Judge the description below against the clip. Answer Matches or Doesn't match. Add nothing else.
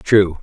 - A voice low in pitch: Matches